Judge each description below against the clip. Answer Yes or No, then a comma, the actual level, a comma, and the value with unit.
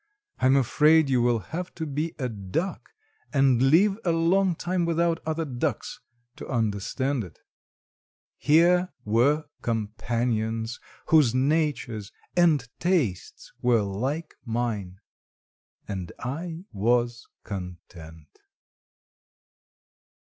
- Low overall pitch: Yes, low, 130 Hz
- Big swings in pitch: Yes, wide, 6.4 semitones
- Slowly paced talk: Yes, slow, 105 wpm